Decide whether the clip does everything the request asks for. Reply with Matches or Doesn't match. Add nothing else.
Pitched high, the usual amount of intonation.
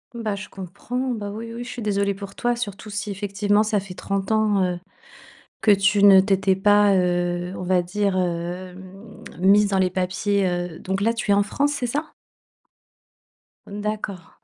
Doesn't match